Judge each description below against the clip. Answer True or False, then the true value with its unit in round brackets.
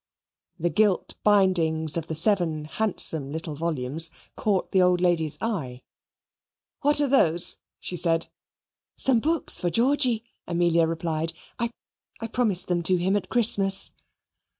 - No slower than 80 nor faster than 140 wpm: True (135 wpm)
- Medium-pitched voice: True (175 Hz)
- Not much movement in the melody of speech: False (4.7 semitones)